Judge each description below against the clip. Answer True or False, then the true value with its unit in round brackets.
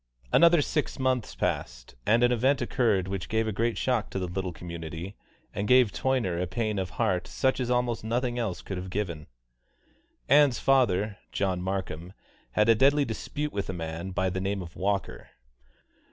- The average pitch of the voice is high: False (105 Hz)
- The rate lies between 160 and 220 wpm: True (180 wpm)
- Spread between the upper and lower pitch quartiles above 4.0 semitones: True (5.1 semitones)